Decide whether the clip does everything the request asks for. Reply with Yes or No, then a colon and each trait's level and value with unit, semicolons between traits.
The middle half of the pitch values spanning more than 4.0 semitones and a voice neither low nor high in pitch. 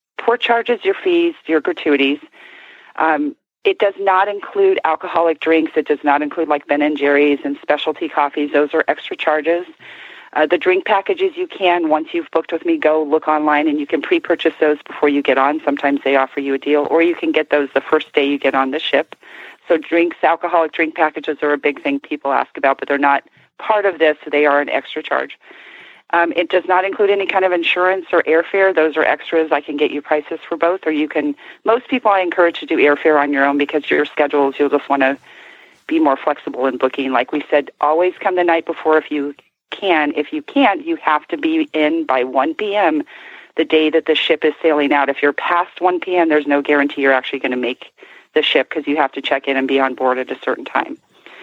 No: average, 3.6 semitones; medium, 155 Hz